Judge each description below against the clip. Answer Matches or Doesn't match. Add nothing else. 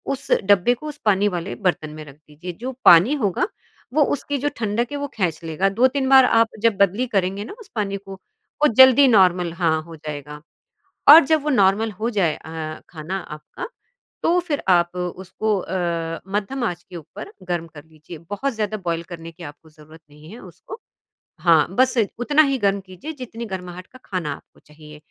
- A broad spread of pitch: Matches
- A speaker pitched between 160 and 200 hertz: Matches